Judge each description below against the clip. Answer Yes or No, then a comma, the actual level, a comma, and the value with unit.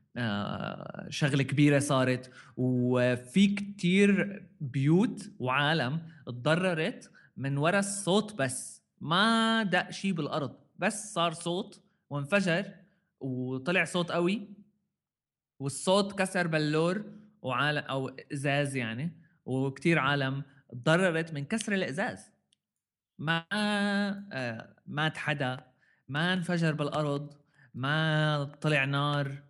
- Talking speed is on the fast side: No, average, 95 wpm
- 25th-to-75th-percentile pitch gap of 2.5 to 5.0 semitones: No, wide, 5.6 semitones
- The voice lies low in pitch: No, medium, 155 Hz